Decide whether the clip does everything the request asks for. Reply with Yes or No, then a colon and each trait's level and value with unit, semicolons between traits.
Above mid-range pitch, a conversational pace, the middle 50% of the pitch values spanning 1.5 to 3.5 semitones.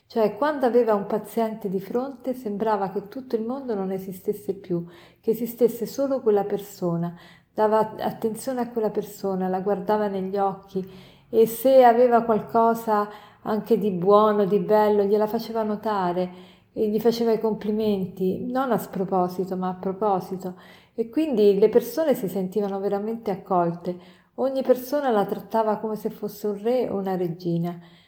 Yes: high, 210 Hz; average, 155 wpm; average, 2.7 semitones